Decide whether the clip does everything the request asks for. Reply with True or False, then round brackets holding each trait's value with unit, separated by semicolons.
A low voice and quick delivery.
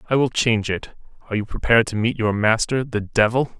True (115 Hz; 215 wpm)